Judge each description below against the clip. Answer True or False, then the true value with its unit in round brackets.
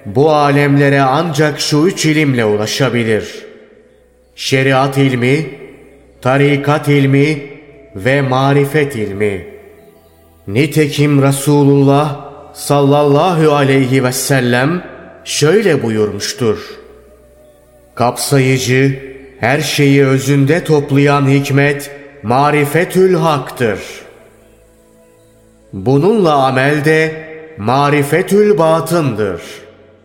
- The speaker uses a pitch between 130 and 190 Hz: True (140 Hz)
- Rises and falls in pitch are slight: True (2.1 semitones)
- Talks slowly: True (70 wpm)